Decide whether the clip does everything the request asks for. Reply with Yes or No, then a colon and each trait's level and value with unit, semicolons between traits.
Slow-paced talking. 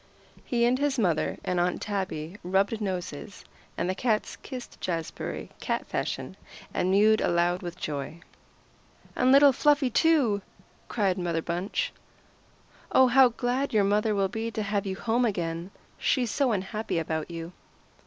No: average, 150 wpm